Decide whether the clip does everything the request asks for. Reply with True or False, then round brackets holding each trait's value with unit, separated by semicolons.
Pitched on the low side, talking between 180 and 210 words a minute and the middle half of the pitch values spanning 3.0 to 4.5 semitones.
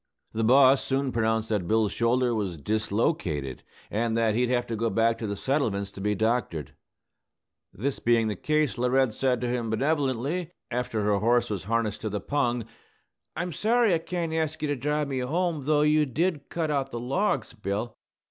False (120 Hz; 185 wpm; 4.9 semitones)